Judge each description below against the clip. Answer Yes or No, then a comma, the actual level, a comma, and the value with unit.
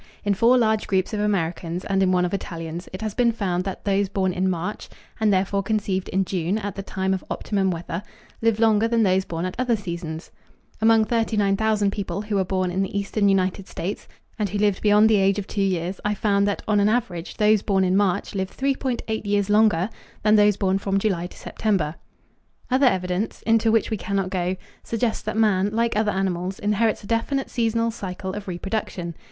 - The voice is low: No, high, 200 Hz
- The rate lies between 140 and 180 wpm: No, fast, 205 wpm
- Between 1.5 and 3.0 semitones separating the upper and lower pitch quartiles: Yes, narrow, 2.5 semitones